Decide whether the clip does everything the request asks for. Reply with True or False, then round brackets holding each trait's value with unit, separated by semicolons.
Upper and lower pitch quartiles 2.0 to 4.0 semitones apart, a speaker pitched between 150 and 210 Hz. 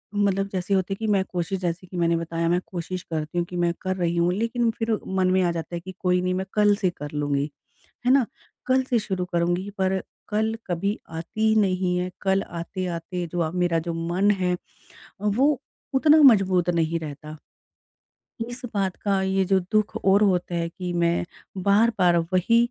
True (2.8 semitones; 185 Hz)